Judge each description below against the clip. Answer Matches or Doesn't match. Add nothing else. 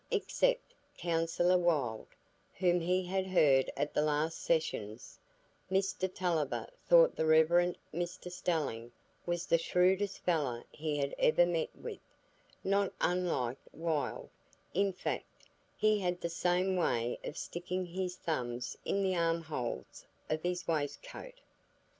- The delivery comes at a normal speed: Doesn't match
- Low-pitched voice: Doesn't match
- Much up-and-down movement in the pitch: Doesn't match